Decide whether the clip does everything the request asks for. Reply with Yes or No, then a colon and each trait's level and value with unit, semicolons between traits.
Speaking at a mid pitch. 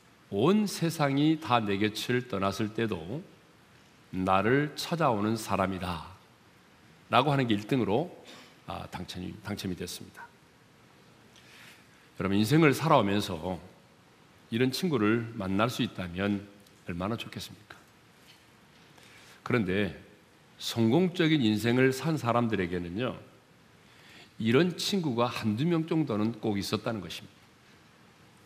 No: low, 110 Hz